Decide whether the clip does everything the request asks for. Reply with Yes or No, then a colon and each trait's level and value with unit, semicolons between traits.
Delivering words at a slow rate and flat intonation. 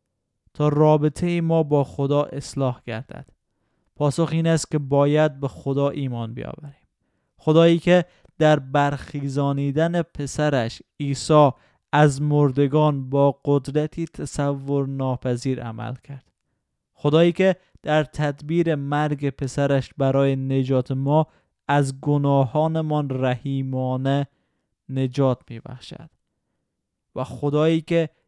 Yes: slow, 100 wpm; narrow, 2.2 semitones